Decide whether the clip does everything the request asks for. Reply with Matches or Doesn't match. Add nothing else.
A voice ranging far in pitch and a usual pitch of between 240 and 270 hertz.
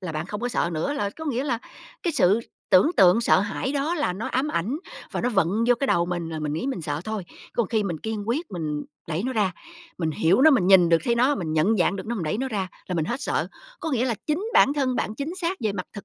Doesn't match